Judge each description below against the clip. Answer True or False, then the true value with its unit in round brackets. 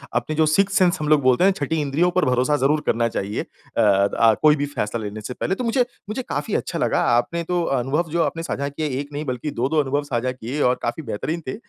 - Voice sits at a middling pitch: True (145 Hz)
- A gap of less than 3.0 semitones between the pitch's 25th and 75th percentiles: False (4.9 semitones)